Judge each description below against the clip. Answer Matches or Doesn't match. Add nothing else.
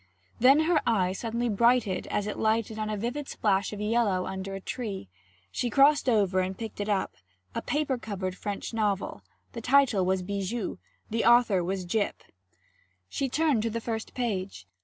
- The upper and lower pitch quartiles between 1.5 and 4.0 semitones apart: Matches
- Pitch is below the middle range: Doesn't match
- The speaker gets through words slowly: Doesn't match